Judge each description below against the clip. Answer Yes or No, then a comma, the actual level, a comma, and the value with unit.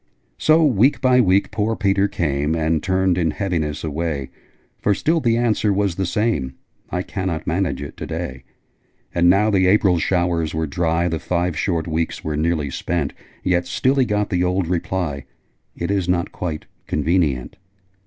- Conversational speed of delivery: Yes, average, 170 wpm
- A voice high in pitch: No, very low, 90 Hz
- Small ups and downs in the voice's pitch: No, average, 3.8 semitones